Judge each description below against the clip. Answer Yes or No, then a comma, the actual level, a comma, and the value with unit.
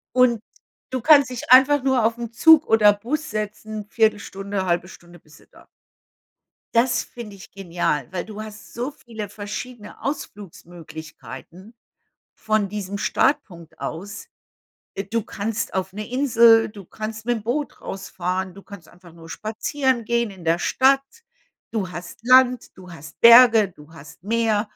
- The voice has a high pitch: Yes, high, 215 Hz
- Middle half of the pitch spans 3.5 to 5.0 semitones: Yes, average, 4.2 semitones